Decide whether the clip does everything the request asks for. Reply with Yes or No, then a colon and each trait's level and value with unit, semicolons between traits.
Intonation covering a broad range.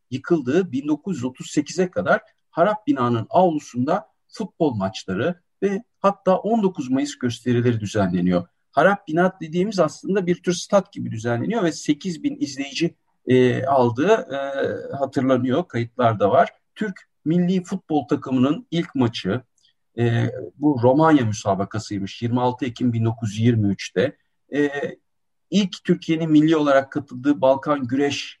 Yes: wide, 6.5 semitones